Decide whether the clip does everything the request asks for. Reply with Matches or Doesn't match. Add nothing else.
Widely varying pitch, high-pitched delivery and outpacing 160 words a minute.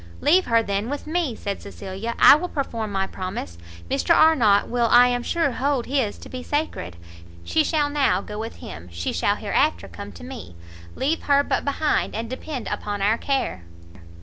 Matches